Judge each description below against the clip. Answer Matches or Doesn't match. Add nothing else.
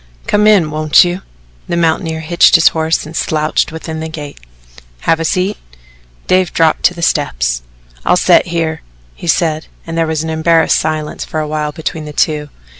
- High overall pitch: Doesn't match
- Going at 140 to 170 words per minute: Doesn't match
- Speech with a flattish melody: Matches